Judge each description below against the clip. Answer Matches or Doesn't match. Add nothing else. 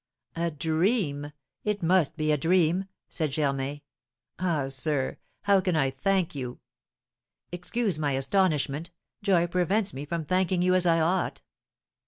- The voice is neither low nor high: Matches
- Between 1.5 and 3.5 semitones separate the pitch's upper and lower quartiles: Doesn't match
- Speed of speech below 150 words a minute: Matches